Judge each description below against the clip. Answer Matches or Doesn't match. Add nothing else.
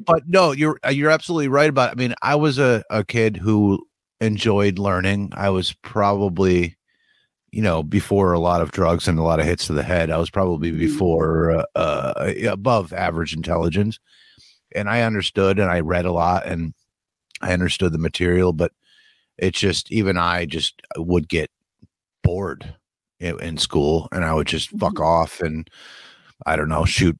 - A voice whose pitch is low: Matches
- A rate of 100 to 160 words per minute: Doesn't match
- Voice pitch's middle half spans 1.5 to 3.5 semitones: Doesn't match